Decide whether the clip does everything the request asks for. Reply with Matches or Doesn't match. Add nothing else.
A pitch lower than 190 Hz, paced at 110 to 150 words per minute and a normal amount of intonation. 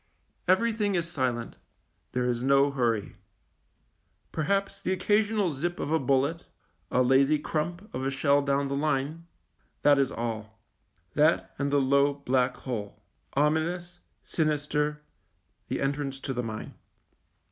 Matches